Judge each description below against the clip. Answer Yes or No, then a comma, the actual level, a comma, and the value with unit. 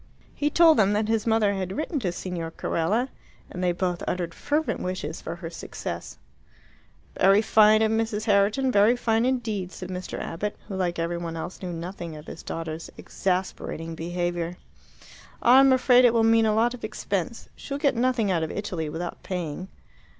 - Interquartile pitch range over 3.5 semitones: Yes, average, 4.6 semitones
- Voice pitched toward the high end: Yes, high, 195 Hz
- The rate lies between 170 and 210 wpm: Yes, average, 180 wpm